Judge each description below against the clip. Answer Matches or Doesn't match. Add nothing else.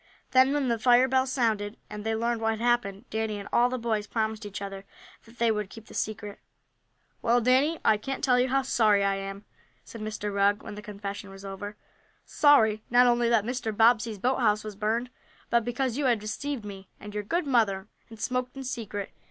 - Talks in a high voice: Matches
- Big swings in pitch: Doesn't match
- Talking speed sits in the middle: Doesn't match